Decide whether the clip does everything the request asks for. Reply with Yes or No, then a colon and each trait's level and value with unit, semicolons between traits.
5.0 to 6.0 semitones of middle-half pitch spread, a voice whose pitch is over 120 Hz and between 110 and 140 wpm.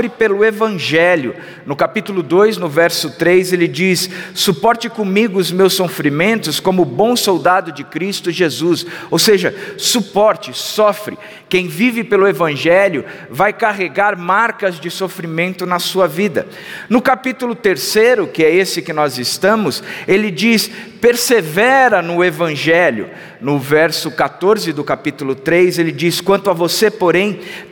No: average, 3.7 semitones; medium, 185 Hz; average, 135 wpm